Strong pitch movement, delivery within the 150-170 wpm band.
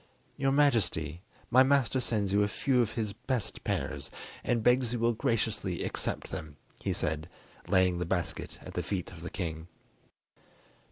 Yes: wide, 5.7 semitones; average, 165 wpm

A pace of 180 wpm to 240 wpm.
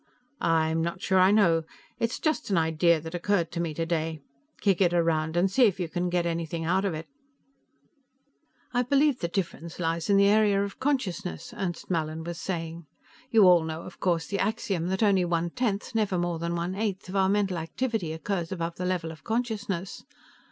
Yes: average, 195 wpm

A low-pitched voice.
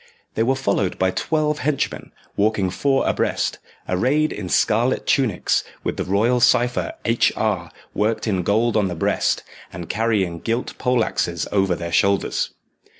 Yes: low, 105 Hz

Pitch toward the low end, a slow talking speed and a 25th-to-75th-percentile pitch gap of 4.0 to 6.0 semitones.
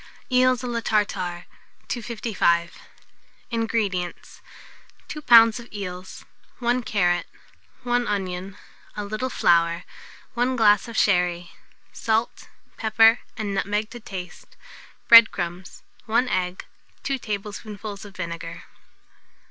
No: high, 210 Hz; slow, 110 wpm; average, 4.3 semitones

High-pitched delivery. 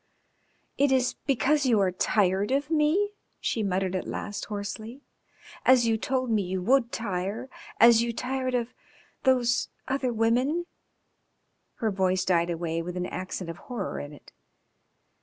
Yes: high, 225 Hz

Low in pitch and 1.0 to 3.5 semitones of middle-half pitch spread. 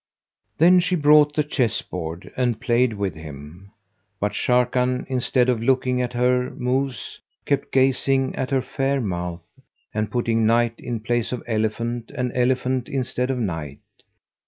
Yes: low, 125 Hz; average, 3.0 semitones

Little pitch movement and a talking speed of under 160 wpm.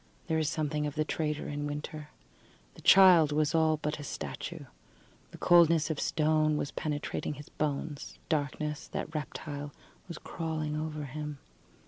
Yes: narrow, 1.2 semitones; average, 150 wpm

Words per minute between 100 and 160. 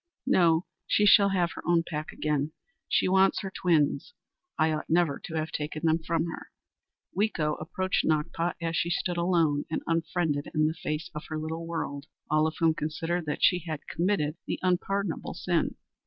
No: average, 180 wpm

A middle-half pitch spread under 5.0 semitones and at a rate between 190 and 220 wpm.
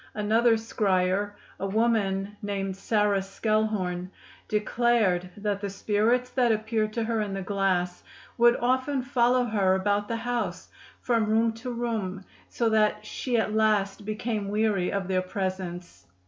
No: average, 2.8 semitones; average, 145 wpm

